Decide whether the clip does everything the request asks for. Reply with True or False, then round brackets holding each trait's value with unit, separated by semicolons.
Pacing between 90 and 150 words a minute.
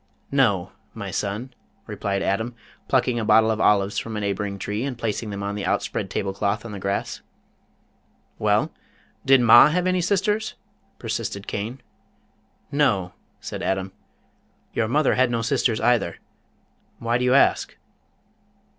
True (145 wpm)